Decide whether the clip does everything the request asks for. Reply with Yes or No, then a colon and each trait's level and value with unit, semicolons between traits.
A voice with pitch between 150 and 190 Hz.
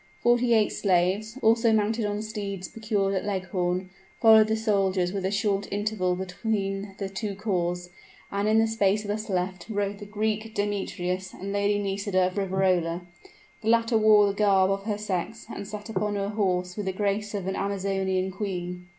No: high, 200 Hz